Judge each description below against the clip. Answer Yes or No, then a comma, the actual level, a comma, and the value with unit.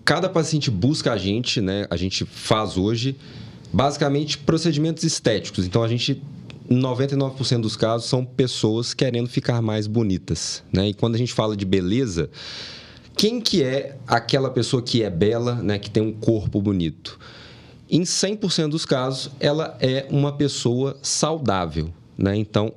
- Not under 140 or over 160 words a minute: Yes, average, 155 wpm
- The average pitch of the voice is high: No, low, 125 Hz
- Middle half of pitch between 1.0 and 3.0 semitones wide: No, average, 4.7 semitones